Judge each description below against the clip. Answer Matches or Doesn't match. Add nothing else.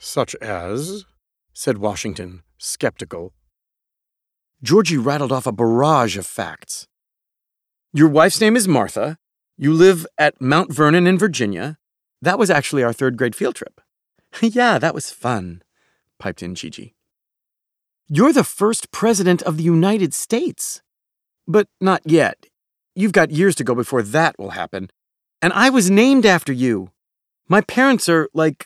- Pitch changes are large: Matches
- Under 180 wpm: Matches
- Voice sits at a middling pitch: Matches